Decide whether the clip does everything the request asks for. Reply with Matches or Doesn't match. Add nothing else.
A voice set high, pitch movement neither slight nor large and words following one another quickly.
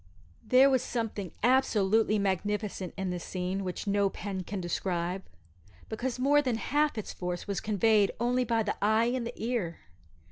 Doesn't match